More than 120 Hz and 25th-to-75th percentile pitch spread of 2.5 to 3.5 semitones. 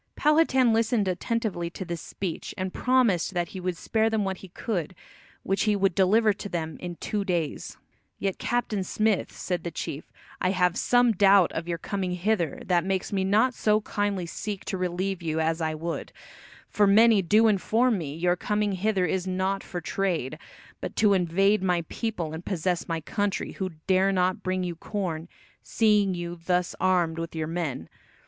Yes: medium, 185 Hz; average, 3.2 semitones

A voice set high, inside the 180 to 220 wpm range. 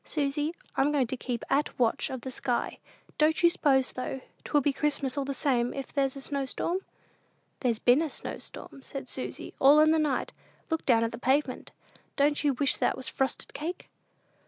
Yes: very high, 275 Hz; average, 190 wpm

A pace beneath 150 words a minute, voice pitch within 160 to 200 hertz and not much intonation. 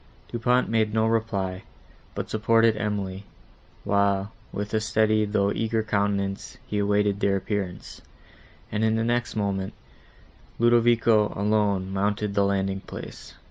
No: slow, 135 wpm; low, 105 Hz; narrow, 2.0 semitones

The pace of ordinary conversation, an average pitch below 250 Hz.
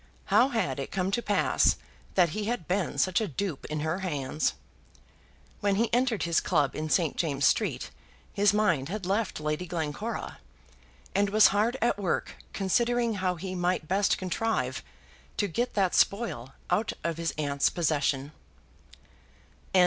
Yes: average, 155 wpm; medium, 185 Hz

